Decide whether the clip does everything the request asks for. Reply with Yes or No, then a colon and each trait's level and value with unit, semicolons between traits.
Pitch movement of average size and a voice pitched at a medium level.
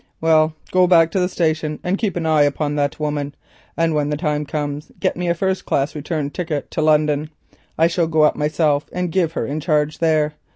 No: narrow, 2.0 semitones; medium, 155 Hz